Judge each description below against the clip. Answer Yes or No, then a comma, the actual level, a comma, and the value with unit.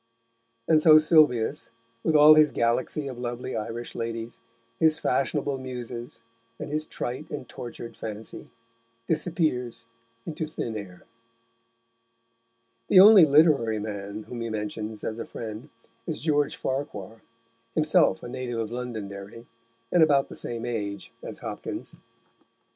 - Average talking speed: No, slow, 130 wpm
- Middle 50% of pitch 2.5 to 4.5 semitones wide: No, average, 5.2 semitones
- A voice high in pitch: No, low, 120 Hz